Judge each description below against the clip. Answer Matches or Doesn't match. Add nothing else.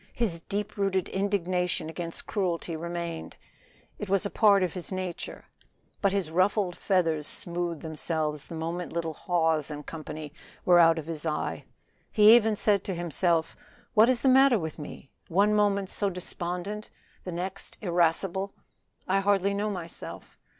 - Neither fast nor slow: Matches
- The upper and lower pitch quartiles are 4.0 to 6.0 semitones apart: Doesn't match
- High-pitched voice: Doesn't match